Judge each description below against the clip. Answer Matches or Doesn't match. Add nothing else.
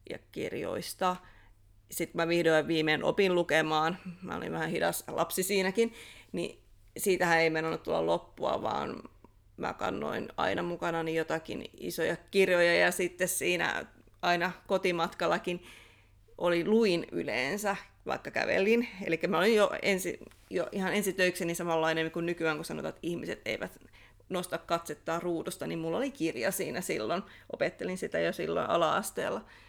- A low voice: Doesn't match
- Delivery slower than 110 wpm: Doesn't match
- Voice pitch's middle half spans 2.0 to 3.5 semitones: Matches